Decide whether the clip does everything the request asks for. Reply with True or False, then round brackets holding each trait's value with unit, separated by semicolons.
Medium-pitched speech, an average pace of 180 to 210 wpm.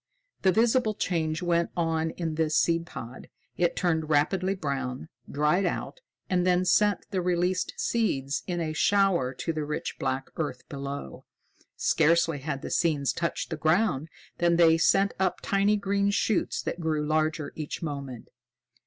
False (165 Hz; 155 wpm)